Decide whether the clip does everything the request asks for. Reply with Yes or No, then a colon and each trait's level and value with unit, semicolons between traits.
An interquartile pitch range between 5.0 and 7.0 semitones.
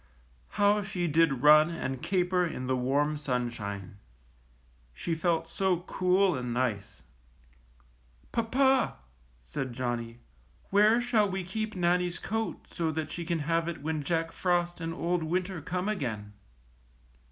Yes: wide, 5.4 semitones